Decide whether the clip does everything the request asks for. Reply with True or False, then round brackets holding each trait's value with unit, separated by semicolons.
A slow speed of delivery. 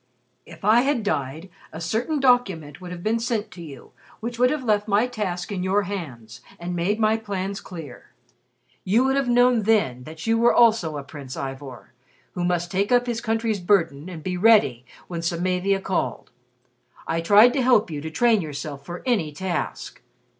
False (185 wpm)